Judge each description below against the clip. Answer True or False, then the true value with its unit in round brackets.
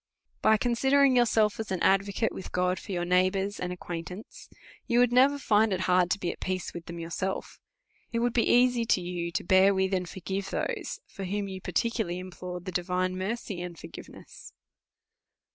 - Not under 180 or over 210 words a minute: True (185 wpm)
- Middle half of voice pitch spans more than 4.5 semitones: False (3.6 semitones)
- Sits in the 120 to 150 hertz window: False (190 Hz)